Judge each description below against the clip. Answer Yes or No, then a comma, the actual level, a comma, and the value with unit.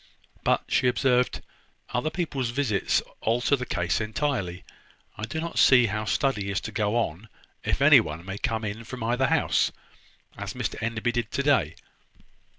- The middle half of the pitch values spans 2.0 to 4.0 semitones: Yes, average, 3.7 semitones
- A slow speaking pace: No, average, 165 wpm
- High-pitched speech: No, low, 115 Hz